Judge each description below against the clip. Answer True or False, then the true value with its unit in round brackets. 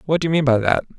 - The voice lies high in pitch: False (140 Hz)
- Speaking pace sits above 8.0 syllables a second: True (8.7 syllables/s)